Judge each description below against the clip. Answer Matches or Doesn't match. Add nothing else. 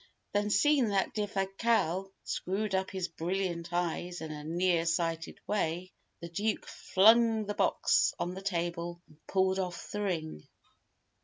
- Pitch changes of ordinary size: Matches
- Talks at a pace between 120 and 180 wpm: Matches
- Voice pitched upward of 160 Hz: Matches